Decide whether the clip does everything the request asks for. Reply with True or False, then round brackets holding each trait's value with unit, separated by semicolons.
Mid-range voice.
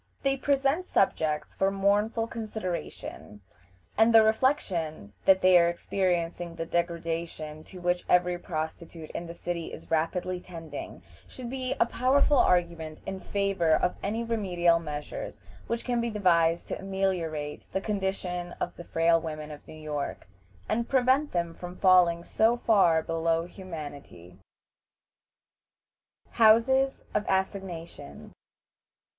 True (180 Hz)